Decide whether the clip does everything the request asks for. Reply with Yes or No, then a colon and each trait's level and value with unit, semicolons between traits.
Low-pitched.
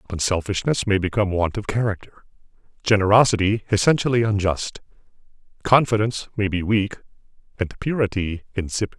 Yes: low, 100 Hz